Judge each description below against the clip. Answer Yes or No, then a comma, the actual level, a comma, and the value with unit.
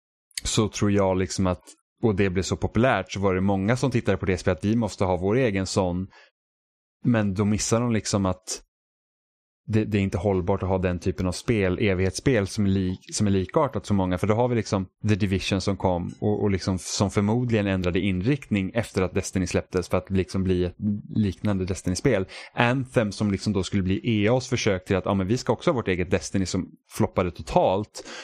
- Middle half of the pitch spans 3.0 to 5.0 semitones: No, narrow, 2.5 semitones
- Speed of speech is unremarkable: No, fast, 215 wpm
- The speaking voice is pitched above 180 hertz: No, low, 100 Hz